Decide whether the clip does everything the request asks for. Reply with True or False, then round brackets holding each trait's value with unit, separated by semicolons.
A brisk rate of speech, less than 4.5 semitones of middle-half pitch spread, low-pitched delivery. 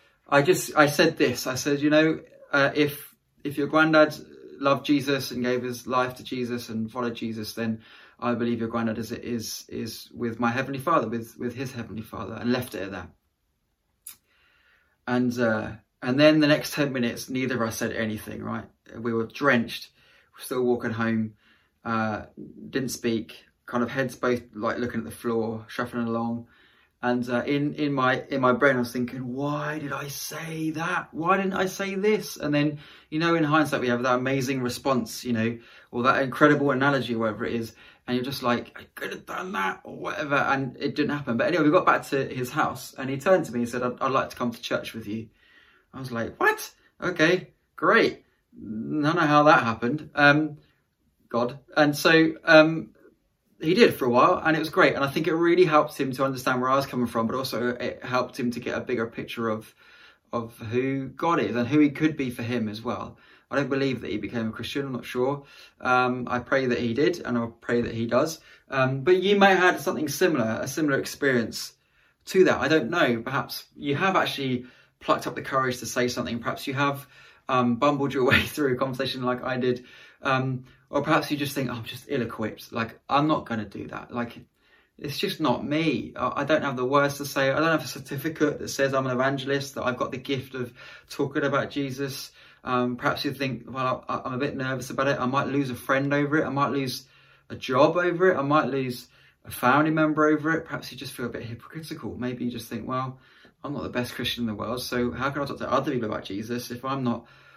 True (225 wpm; 3.2 semitones; 130 Hz)